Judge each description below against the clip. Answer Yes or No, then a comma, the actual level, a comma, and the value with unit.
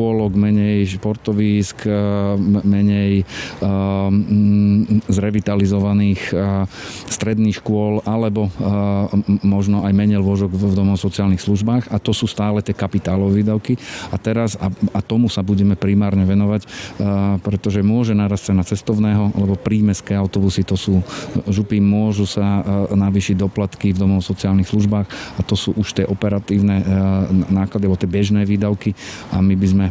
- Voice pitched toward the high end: No, low, 100 Hz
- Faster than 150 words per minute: No, average, 130 wpm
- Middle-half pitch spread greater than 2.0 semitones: No, narrow, 1.1 semitones